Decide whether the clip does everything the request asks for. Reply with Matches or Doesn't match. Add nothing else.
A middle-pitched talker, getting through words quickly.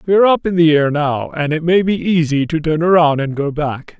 Matches